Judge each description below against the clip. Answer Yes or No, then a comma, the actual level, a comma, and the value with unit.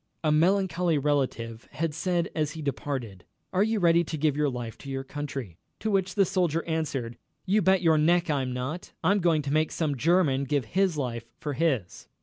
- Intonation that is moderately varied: Yes, average, 4.4 semitones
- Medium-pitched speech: Yes, medium, 155 Hz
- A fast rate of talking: No, average, 195 wpm